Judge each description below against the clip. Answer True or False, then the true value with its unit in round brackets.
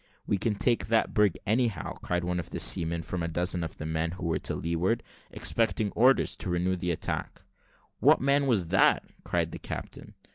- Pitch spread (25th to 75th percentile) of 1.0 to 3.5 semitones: False (4.6 semitones)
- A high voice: False (90 Hz)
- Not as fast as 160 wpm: False (195 wpm)